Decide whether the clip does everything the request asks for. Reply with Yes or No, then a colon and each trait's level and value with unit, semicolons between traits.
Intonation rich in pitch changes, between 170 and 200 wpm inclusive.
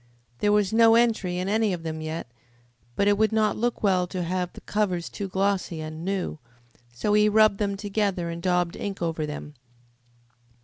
No: average, 3.5 semitones; average, 185 wpm